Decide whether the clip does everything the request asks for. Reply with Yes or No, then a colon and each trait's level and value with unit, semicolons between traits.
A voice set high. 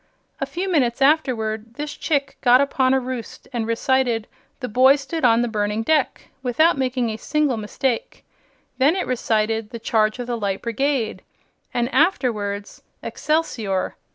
Yes: high, 245 Hz